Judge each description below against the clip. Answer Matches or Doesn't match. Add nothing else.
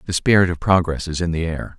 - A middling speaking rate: Doesn't match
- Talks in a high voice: Doesn't match